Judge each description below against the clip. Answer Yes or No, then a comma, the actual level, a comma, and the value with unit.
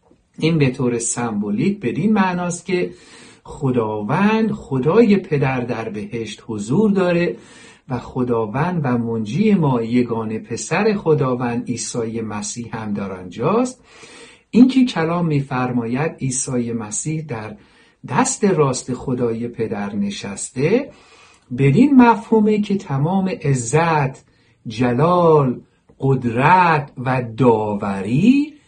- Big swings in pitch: Yes, wide, 8.0 semitones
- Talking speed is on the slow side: Yes, slow, 100 wpm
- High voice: No, low, 135 Hz